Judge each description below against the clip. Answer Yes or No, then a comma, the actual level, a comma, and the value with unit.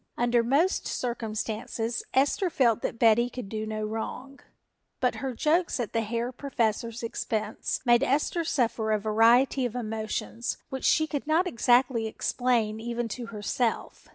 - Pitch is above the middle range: Yes, high, 235 Hz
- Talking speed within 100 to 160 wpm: Yes, average, 150 wpm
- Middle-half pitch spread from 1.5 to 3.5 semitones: Yes, average, 2.9 semitones